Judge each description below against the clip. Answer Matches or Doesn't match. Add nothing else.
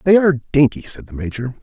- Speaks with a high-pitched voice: Doesn't match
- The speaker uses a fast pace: Matches